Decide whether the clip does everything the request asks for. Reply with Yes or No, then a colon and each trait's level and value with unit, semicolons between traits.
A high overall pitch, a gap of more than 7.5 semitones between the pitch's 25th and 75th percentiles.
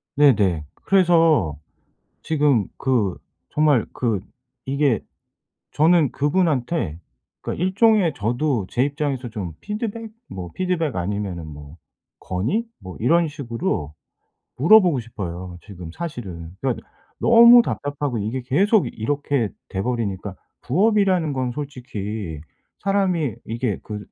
No: low, 130 Hz; wide, 8.4 semitones